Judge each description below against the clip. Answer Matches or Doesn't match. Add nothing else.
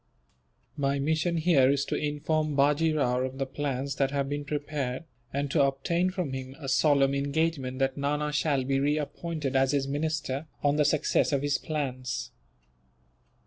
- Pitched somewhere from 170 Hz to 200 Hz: Doesn't match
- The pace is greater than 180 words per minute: Doesn't match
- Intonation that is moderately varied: Doesn't match